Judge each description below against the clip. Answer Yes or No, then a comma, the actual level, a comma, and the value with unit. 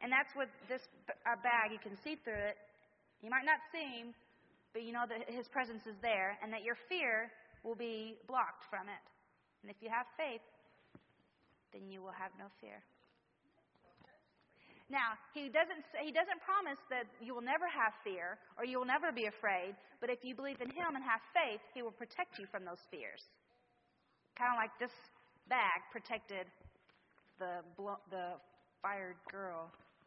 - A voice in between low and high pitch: No, high, 230 Hz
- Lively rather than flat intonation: No, average, 4.0 semitones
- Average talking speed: Yes, average, 175 wpm